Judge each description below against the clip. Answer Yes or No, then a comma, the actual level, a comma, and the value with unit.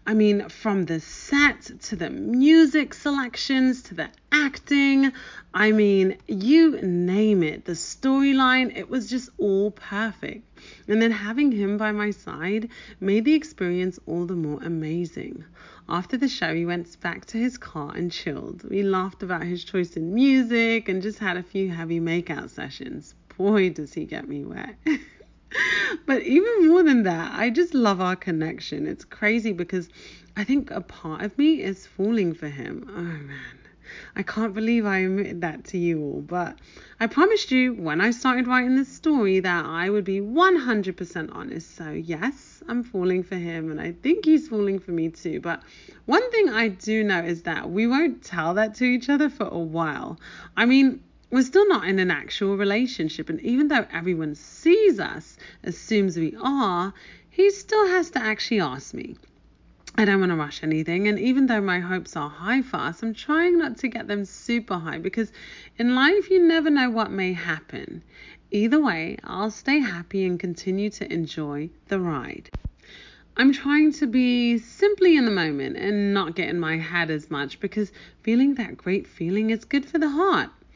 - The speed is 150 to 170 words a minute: No, average, 185 wpm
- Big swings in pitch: Yes, wide, 6.7 semitones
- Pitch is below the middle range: No, high, 210 Hz